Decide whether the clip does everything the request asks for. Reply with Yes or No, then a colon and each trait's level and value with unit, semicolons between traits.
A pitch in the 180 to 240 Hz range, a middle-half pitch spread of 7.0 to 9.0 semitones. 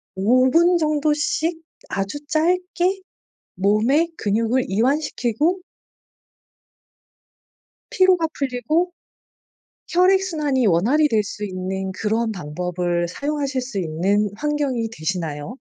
No: very high, 250 Hz; wide, 7.8 semitones